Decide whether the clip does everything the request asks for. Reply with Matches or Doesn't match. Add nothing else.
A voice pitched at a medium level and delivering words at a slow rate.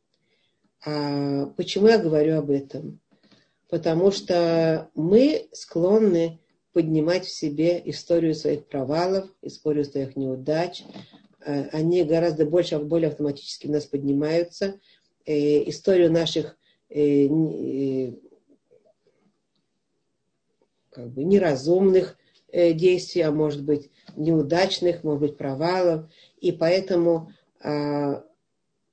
Matches